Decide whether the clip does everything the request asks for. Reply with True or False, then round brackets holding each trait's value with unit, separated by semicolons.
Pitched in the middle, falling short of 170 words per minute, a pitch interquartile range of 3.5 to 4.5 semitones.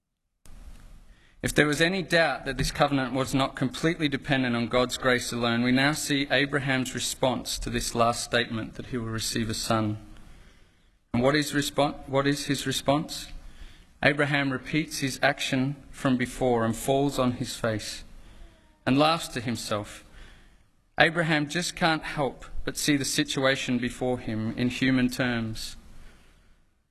False (130 Hz; 150 wpm; 3.9 semitones)